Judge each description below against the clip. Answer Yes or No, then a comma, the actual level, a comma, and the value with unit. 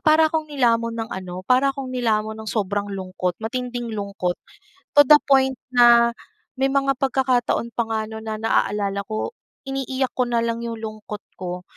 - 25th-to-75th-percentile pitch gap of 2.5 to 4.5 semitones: Yes, average, 3.6 semitones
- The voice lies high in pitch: Yes, high, 230 Hz